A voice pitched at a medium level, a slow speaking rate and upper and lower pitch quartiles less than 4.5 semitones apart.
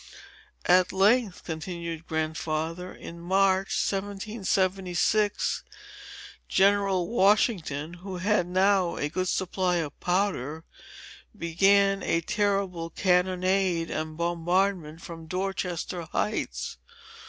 Yes: medium, 180 Hz; slow, 90 wpm; average, 2.8 semitones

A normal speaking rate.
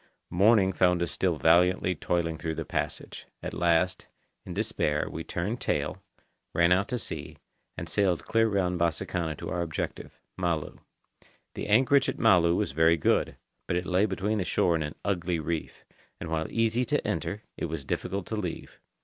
Yes: average, 175 wpm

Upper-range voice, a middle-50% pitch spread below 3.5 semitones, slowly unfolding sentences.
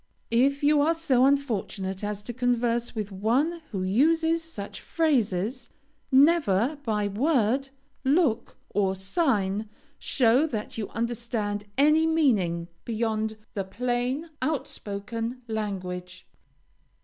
No: high, 235 Hz; wide, 5.4 semitones; slow, 110 wpm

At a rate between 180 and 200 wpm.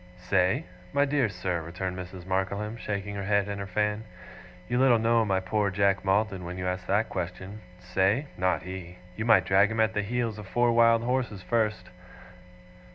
Yes: average, 185 wpm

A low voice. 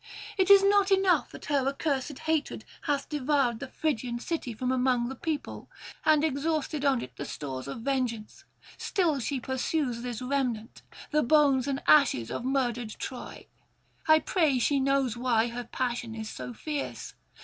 No: very high, 265 Hz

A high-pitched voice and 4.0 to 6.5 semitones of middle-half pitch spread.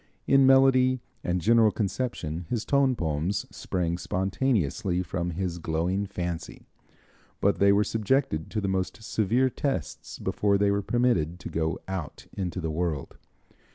No: very low, 95 Hz; average, 5.1 semitones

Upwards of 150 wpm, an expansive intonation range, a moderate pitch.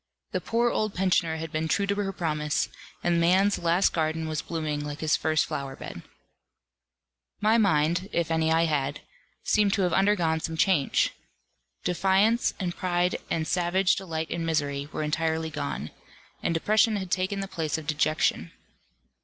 No: average, 160 wpm; average, 3.5 semitones; medium, 165 Hz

